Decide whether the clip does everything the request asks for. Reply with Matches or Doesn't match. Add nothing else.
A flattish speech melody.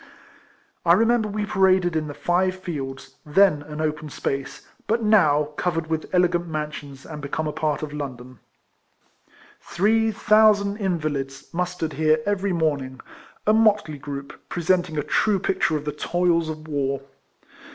Doesn't match